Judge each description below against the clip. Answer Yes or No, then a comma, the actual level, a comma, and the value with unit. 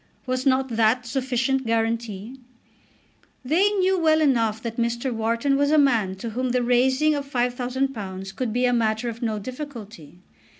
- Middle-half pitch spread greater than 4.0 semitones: No, average, 3.0 semitones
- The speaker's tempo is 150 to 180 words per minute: Yes, average, 160 wpm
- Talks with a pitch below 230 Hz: No, high, 245 Hz